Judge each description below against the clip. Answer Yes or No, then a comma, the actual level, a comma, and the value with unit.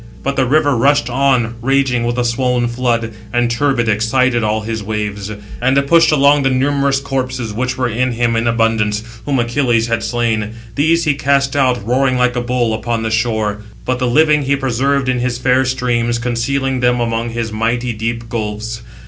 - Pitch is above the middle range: No, low, 120 Hz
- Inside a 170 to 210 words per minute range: Yes, average, 195 wpm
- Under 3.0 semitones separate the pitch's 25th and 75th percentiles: Yes, narrow, 2.5 semitones